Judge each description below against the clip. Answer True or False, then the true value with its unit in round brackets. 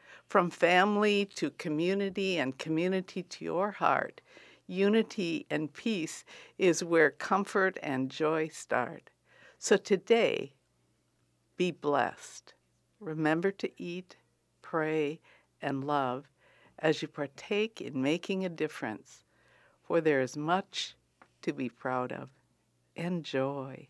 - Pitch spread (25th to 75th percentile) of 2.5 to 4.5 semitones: False (5.5 semitones)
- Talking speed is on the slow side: True (110 wpm)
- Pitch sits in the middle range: True (160 Hz)